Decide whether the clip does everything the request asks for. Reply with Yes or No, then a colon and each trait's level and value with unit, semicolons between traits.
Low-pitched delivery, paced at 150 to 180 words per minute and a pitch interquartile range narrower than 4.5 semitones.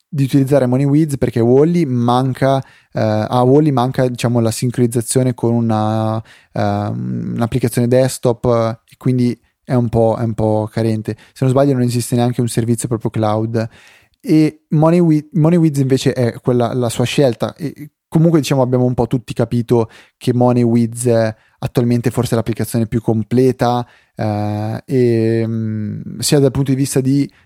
Yes: low, 120 Hz; average, 160 wpm; average, 2.9 semitones